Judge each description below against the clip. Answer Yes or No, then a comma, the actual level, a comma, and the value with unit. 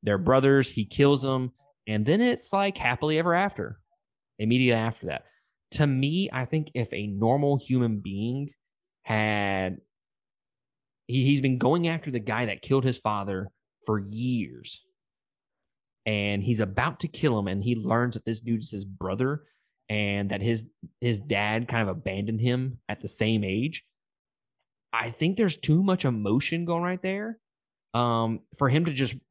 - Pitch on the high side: No, low, 125 Hz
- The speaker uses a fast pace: No, average, 165 wpm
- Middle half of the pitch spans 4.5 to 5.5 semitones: Yes, average, 4.8 semitones